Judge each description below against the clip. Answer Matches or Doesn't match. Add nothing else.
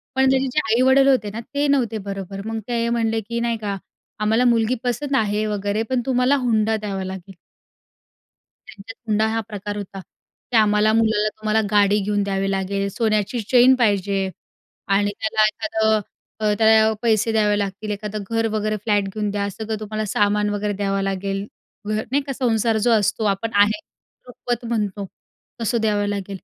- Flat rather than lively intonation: Matches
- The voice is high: Matches